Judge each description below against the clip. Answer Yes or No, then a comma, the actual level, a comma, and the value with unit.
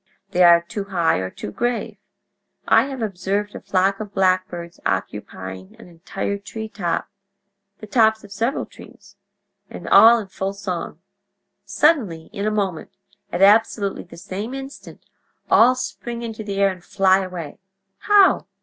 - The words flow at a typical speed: No, slow, 130 wpm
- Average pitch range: Yes, average, 3.1 semitones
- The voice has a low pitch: No, high, 195 Hz